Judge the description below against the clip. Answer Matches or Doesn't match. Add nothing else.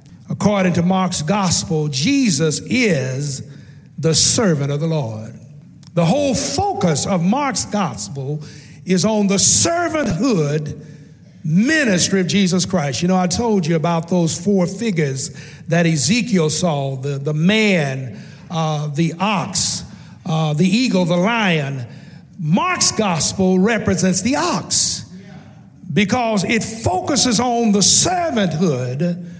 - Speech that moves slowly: Matches